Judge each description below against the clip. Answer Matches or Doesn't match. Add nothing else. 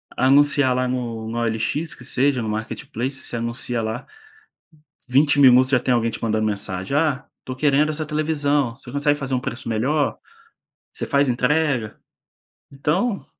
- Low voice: Matches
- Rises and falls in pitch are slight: Doesn't match